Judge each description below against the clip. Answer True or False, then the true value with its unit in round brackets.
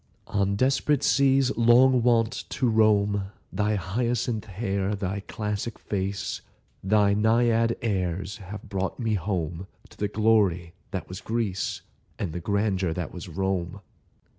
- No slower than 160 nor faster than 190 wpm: False (135 wpm)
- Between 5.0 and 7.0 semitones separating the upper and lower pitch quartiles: False (3.1 semitones)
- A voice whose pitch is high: False (105 Hz)